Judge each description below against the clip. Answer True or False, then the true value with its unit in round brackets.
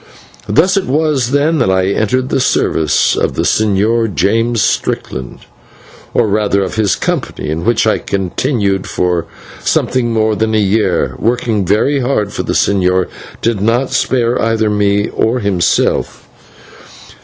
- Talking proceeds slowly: False (145 wpm)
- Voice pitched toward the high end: False (110 Hz)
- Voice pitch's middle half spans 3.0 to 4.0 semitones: True (3.5 semitones)